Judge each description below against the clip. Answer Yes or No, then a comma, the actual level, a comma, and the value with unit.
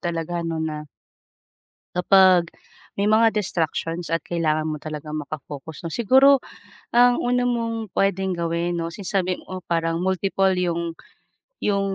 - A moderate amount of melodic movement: Yes, average, 3.2 semitones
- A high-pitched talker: No, medium, 175 Hz